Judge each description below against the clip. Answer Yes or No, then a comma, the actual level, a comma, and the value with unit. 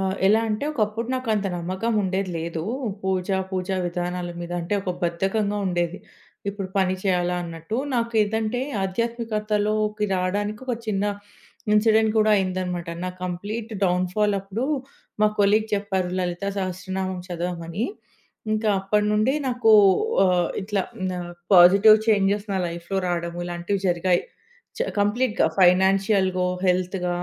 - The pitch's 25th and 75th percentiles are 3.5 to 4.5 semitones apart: No, average, 3.0 semitones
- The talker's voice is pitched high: Yes, high, 195 Hz